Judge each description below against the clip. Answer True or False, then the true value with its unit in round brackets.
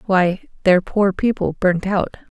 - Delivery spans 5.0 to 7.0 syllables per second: False (4.3 syllables/s)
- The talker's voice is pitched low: False (190 Hz)